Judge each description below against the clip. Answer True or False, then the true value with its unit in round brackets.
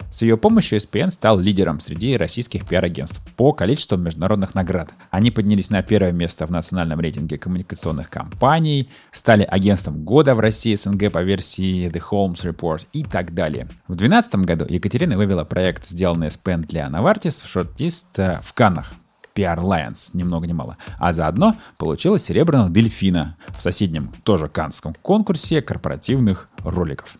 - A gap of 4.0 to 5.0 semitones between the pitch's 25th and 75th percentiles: True (4.3 semitones)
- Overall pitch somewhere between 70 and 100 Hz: True (95 Hz)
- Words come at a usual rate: True (150 wpm)